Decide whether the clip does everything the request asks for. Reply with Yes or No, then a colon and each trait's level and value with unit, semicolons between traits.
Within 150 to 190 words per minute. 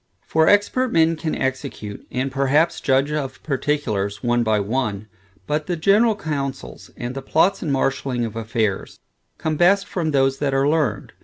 Yes: average, 165 wpm